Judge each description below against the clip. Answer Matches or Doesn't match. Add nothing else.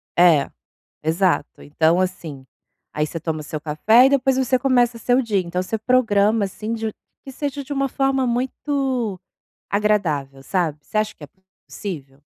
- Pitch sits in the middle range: Doesn't match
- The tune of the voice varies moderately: Doesn't match